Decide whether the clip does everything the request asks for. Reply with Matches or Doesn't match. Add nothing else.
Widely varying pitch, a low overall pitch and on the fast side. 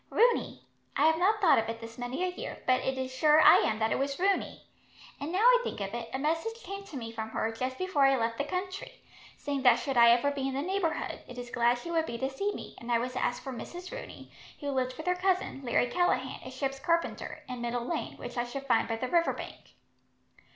Doesn't match